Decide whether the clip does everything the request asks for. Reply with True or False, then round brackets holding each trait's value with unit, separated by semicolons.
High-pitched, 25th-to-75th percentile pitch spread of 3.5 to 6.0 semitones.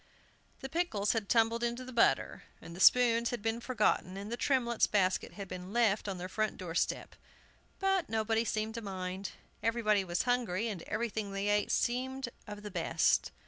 False (220 Hz; 3.1 semitones)